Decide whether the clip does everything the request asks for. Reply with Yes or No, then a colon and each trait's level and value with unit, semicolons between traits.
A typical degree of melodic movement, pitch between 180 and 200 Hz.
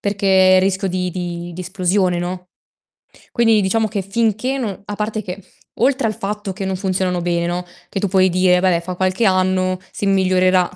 No: narrow, 1.8 semitones; medium, 185 Hz